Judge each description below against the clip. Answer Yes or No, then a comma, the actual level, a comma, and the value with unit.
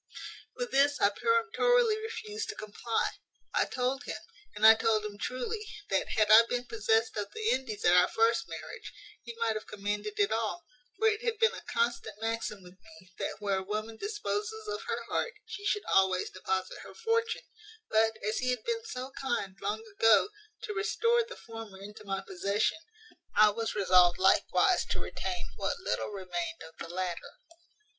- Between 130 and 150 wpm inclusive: No, average, 180 wpm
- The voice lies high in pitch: Yes, high, 225 Hz